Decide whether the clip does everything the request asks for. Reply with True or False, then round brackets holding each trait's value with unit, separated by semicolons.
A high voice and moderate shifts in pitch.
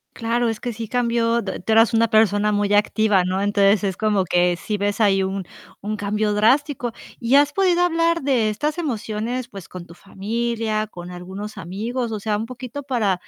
True (215 Hz; 3.0 semitones)